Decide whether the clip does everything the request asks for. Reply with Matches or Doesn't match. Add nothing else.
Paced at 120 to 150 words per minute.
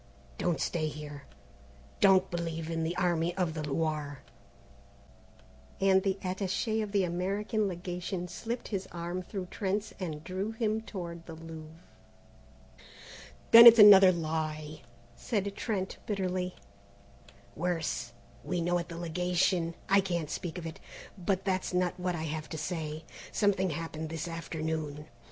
Matches